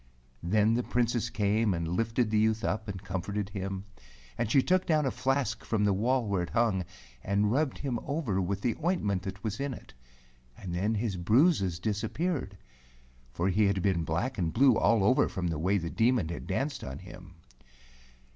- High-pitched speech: No, low, 105 Hz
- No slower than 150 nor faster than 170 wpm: No, average, 195 wpm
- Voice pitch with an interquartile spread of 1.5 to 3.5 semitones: No, average, 4.3 semitones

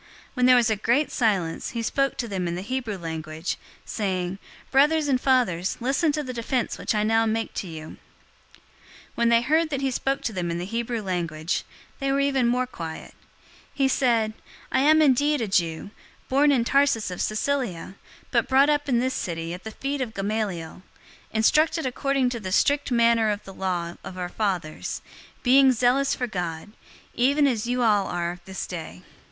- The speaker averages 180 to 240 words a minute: Yes, average, 190 wpm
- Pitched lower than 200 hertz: No, high, 230 Hz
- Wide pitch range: Yes, wide, 6.3 semitones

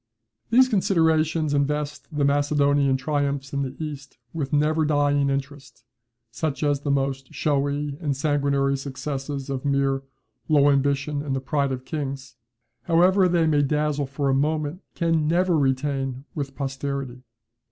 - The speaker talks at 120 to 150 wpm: Yes, average, 145 wpm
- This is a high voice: No, medium, 145 Hz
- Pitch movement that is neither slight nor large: No, narrow, 1.7 semitones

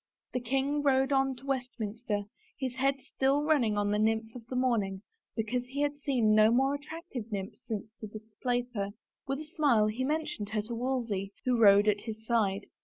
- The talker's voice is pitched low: No, high, 240 Hz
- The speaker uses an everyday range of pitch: Yes, average, 4.0 semitones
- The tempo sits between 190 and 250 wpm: Yes, average, 195 wpm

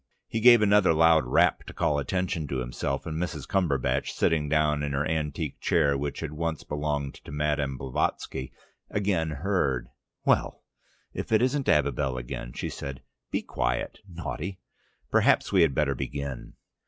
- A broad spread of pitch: No, average, 3.3 semitones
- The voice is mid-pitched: No, very low, 75 Hz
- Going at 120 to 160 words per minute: Yes, average, 155 wpm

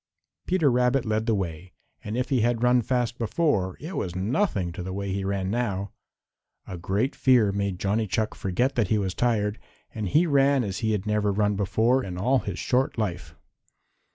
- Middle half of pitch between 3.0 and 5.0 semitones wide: Yes, average, 4.2 semitones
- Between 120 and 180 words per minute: No, average, 195 wpm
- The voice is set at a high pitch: No, low, 110 Hz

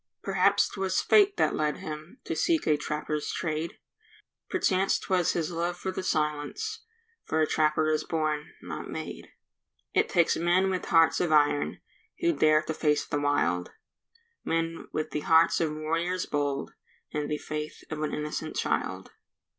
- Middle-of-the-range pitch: Yes, medium, 155 Hz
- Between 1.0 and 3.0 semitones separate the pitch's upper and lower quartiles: Yes, average, 2.7 semitones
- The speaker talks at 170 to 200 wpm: No, average, 155 wpm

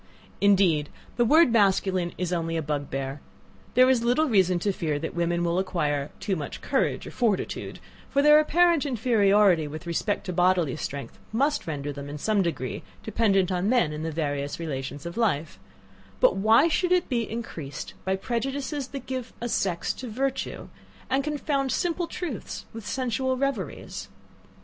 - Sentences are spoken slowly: No, average, 165 wpm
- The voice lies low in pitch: No, high, 195 Hz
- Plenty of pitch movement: Yes, wide, 7.9 semitones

